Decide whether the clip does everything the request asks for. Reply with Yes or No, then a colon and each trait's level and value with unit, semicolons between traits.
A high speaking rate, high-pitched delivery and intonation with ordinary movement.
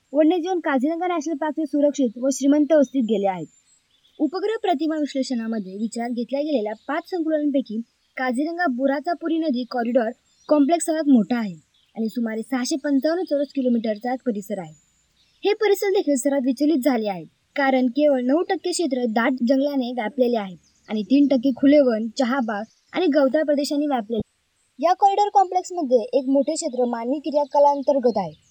Yes: fast, 150 wpm; very high, 275 Hz; average, 4.4 semitones